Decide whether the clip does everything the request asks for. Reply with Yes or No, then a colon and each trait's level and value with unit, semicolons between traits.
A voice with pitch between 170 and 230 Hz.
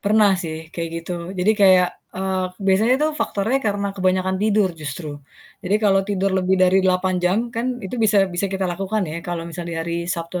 Yes: high, 190 Hz